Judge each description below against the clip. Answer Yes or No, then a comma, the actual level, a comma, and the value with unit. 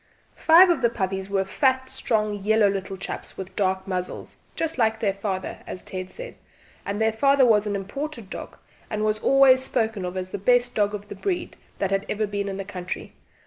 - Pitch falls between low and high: No, high, 210 Hz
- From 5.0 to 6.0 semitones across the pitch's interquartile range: No, average, 4.2 semitones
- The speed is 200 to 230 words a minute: Yes, fast, 205 wpm